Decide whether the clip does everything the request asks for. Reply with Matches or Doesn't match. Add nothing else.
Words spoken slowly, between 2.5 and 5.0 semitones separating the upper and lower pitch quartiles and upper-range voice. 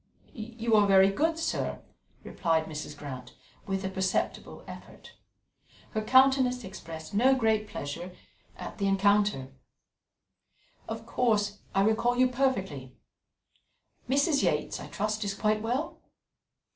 Matches